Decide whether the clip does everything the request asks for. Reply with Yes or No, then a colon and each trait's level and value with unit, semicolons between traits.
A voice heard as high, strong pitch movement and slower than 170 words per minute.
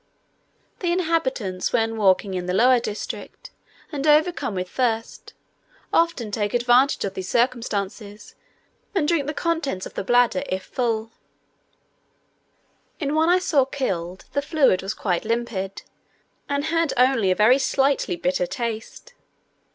Yes: high, 240 Hz; wide, 6.2 semitones; slow, 135 wpm